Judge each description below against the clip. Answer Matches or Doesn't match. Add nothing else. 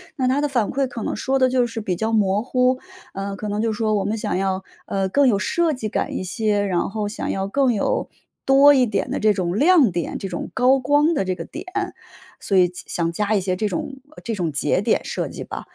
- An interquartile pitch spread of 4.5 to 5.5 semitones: Matches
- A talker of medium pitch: Doesn't match